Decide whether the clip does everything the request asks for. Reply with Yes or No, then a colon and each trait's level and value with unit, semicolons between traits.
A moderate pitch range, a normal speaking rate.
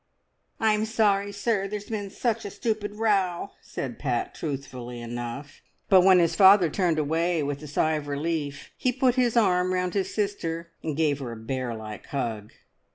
No: wide, 6.5 semitones; average, 175 wpm